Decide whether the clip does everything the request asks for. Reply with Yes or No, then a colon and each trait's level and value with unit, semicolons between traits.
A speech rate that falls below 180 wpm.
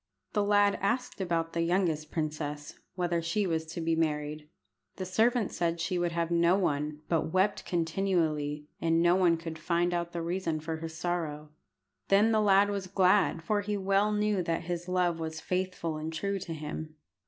No: average, 185 wpm